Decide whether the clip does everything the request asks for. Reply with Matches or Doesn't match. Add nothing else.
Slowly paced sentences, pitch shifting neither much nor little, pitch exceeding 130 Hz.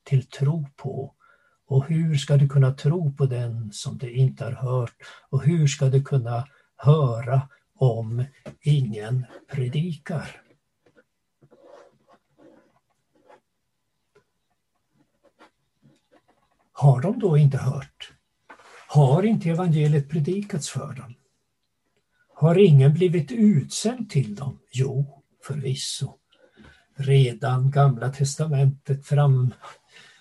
Doesn't match